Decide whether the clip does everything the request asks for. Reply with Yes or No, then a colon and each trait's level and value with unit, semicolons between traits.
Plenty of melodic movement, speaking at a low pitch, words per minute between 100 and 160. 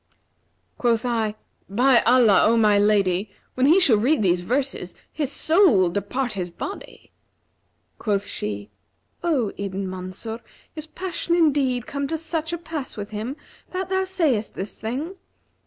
No: wide, 7.4 semitones; high, 240 Hz; average, 150 wpm